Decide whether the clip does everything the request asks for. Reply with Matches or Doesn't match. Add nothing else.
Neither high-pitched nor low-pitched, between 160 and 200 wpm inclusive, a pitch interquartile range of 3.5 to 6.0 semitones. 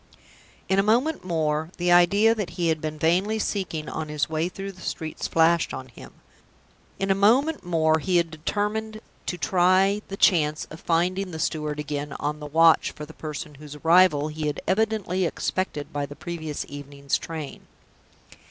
Matches